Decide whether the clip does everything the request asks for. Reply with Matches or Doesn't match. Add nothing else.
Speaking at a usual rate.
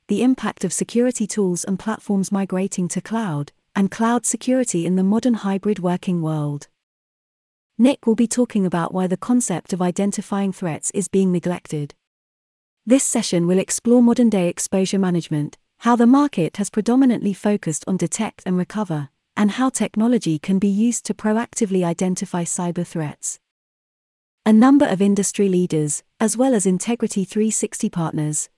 Matches